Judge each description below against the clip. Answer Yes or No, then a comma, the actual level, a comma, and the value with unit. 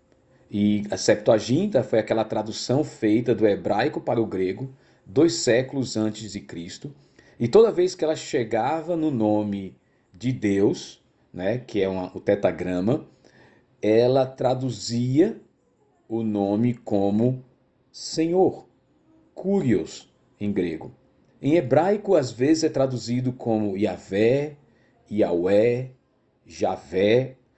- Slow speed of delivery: Yes, slow, 115 wpm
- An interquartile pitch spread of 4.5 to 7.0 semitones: No, average, 4.0 semitones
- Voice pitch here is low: Yes, low, 120 Hz